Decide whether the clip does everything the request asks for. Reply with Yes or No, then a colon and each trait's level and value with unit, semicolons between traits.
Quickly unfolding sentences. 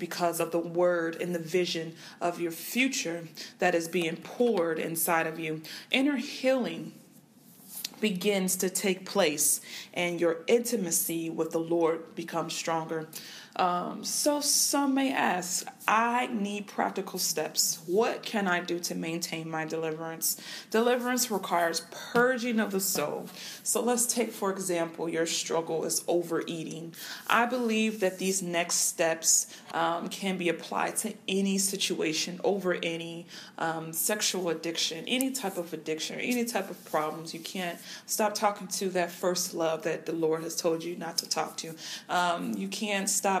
No: average, 155 wpm